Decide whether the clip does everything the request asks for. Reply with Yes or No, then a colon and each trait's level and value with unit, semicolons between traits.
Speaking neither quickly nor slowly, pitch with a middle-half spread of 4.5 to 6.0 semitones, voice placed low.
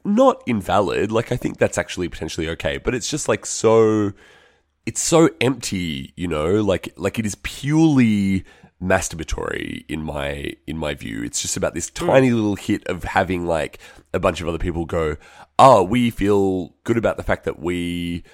Yes: average, 180 wpm; average, 5.3 semitones; low, 100 Hz